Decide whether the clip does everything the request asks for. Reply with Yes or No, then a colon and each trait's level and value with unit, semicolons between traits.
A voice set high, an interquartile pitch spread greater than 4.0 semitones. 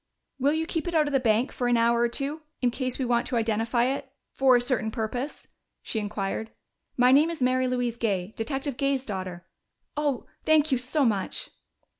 No: very high, 250 Hz; average, 3.3 semitones